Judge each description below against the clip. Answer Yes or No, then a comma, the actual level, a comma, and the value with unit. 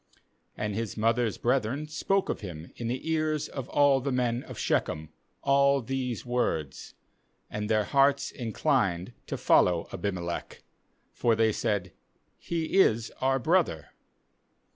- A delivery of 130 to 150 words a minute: Yes, slow, 135 wpm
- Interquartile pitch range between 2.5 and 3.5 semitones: No, average, 4.7 semitones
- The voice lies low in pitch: Yes, low, 120 Hz